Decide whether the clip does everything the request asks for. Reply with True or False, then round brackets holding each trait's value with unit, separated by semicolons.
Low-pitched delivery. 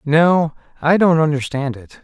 False (155 Hz)